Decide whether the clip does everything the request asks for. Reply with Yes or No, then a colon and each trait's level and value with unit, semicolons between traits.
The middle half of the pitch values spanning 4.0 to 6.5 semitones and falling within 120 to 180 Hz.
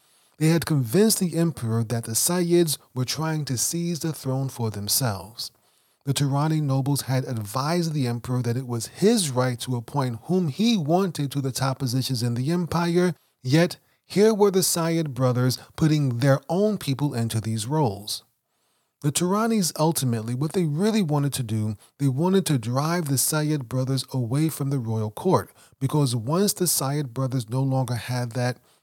Yes: average, 4.7 semitones; medium, 140 Hz